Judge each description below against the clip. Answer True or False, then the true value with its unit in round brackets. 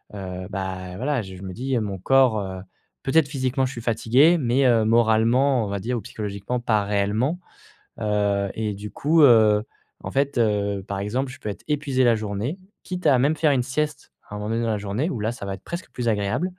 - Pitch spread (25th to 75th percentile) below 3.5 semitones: False (4.7 semitones)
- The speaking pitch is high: False (115 Hz)